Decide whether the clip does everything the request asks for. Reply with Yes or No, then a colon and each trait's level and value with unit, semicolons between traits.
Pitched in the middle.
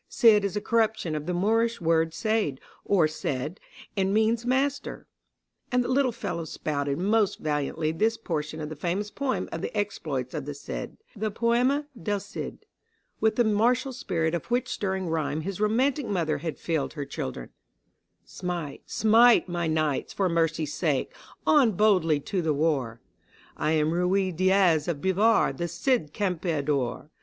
Yes: medium, 180 Hz